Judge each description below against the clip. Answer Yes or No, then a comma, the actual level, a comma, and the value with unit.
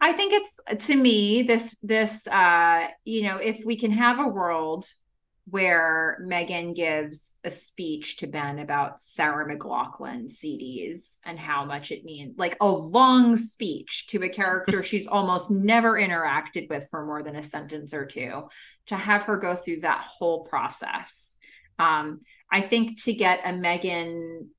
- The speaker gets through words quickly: No, average, 160 wpm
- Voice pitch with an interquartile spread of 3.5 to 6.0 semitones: Yes, average, 5.3 semitones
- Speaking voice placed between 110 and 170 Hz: No, medium, 185 Hz